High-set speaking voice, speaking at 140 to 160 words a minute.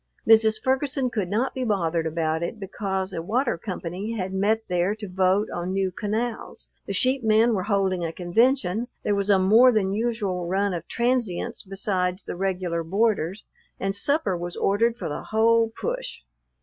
No: high, 200 Hz; average, 175 wpm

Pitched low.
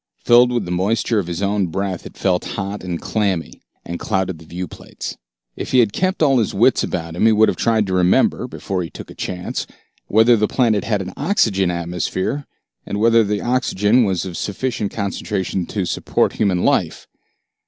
Yes: low, 100 Hz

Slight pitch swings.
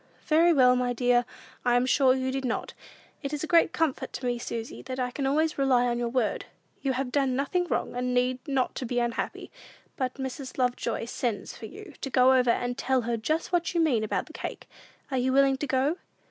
Yes: narrow, 2.1 semitones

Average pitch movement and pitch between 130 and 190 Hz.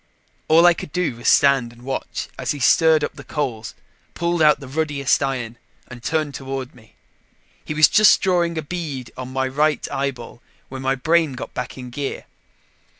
Yes: average, 3.6 semitones; medium, 140 Hz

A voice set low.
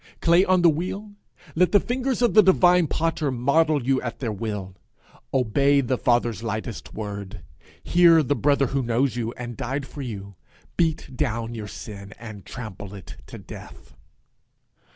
Yes: low, 130 Hz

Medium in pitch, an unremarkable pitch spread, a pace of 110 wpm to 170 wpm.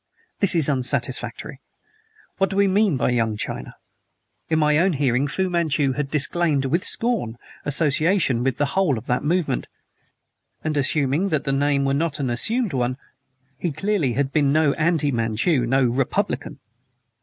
Yes: medium, 145 Hz; average, 4.2 semitones; average, 165 wpm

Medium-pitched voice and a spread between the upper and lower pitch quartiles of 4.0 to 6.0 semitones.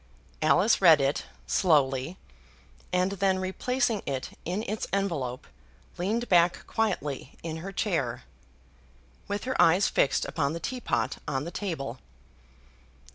Yes: medium, 180 Hz; wide, 5.6 semitones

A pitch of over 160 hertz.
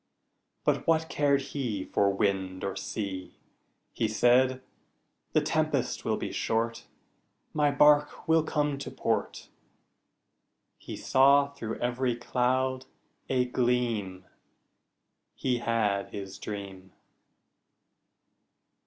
No: low, 125 Hz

